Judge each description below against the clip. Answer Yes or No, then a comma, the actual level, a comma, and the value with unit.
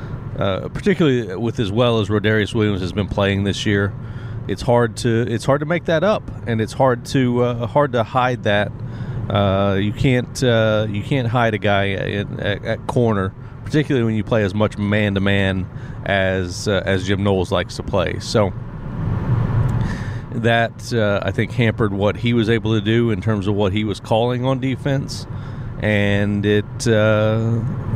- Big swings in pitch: No, average, 3.2 semitones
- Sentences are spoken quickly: No, average, 180 wpm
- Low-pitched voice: Yes, low, 115 Hz